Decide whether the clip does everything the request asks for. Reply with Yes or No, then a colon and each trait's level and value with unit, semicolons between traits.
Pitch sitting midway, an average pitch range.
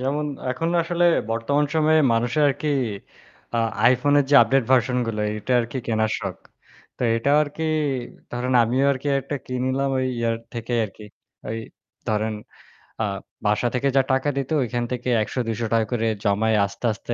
No: low, 125 Hz; average, 3.2 semitones